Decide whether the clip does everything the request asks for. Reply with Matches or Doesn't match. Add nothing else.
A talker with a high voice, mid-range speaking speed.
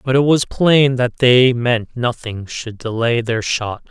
Doesn't match